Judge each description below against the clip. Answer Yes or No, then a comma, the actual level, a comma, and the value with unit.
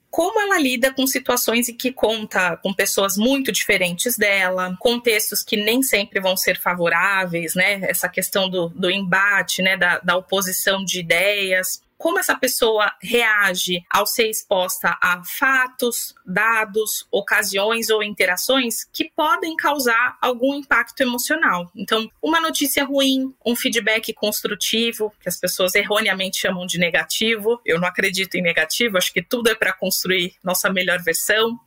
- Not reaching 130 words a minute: No, average, 150 wpm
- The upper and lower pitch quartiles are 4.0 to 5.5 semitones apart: Yes, average, 4.6 semitones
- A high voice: Yes, high, 210 Hz